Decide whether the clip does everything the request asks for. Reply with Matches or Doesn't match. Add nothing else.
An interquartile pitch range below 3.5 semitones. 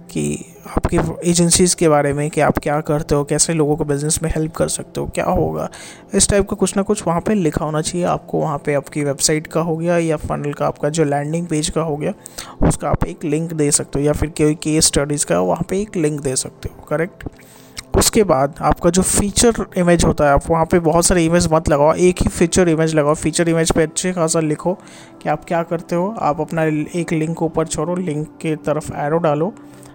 Matches